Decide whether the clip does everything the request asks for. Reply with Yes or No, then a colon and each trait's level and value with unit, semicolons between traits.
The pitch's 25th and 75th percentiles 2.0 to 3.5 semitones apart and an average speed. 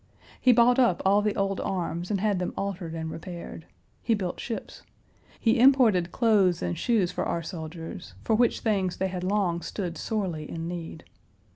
No: average, 4.0 semitones; average, 175 wpm